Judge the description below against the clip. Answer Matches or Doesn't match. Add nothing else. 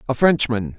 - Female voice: Doesn't match